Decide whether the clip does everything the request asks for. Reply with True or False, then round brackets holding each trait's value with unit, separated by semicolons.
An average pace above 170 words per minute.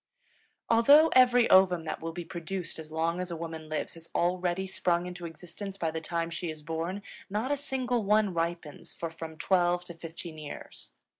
True (190 wpm)